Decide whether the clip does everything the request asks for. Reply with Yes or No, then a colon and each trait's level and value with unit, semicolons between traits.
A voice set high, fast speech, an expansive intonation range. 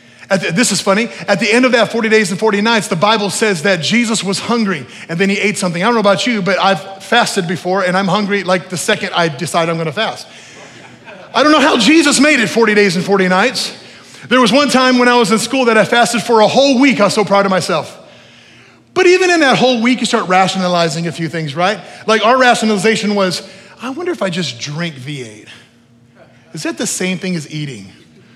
No: high, 200 Hz; fast, 240 wpm; average, 4.2 semitones